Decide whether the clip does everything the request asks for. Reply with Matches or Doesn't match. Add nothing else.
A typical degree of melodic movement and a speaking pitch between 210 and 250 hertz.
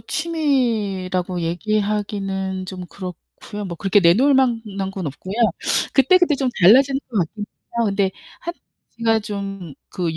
Doesn't match